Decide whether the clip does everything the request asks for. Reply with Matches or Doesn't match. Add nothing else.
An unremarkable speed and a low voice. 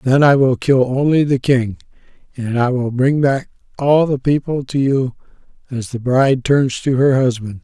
Matches